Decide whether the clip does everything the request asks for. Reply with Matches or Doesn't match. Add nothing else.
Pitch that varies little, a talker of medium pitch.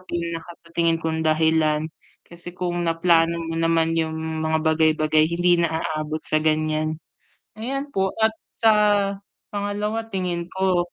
Matches